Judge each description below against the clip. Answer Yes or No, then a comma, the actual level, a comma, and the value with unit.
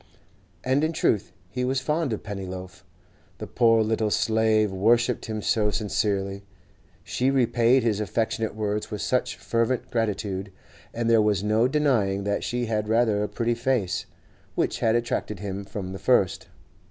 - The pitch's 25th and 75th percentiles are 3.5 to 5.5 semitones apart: No, average, 2.8 semitones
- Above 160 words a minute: No, average, 155 wpm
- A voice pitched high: No, low, 110 Hz